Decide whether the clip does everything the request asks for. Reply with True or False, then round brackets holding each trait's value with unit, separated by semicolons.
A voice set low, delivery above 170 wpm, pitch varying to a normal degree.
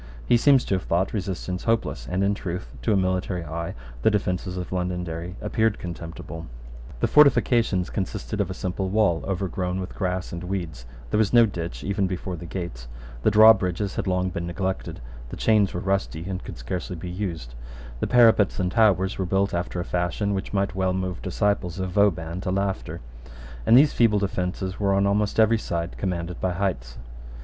False (95 Hz; 185 wpm; 2.3 semitones)